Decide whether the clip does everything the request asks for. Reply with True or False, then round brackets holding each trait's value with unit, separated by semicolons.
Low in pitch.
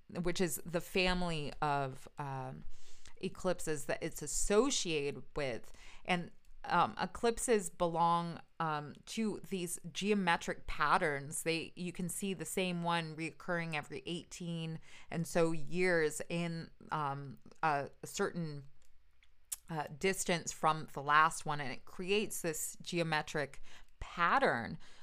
False (170 Hz)